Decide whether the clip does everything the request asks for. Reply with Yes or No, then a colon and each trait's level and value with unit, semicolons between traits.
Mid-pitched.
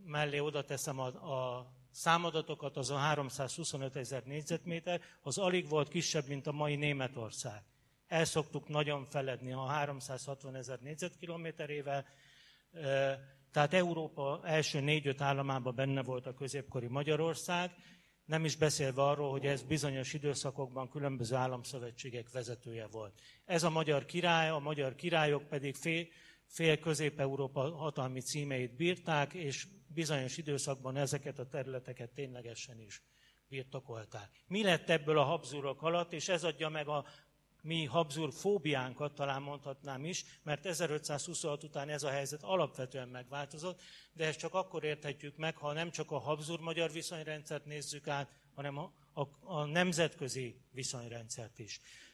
Yes: medium, 145 Hz